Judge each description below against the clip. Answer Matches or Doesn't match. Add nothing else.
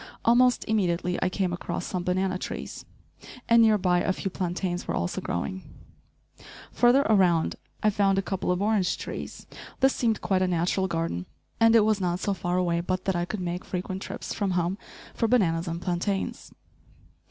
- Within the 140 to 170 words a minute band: Doesn't match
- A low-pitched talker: Doesn't match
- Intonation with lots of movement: Doesn't match